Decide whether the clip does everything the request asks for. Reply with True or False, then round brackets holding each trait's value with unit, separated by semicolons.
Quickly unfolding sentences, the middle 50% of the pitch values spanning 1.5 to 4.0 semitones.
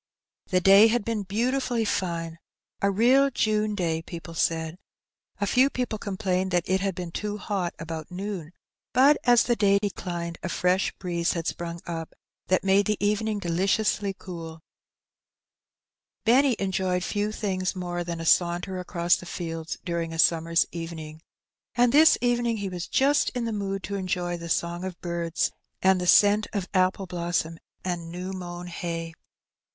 False (165 wpm; 3.4 semitones)